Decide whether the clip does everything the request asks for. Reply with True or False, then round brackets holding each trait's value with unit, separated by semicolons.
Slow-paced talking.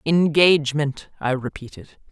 True (85 wpm)